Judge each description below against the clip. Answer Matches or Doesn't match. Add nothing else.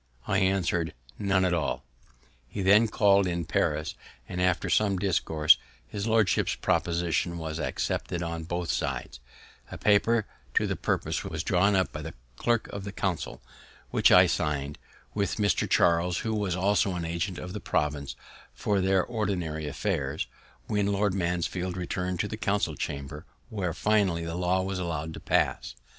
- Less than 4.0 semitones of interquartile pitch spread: Matches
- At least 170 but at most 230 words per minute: Doesn't match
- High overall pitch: Doesn't match